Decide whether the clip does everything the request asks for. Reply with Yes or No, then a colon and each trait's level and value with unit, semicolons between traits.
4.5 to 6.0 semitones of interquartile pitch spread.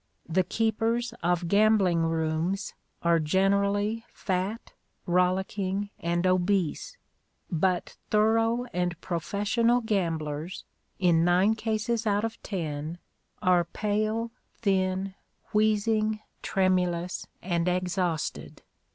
No: average, 3.7 semitones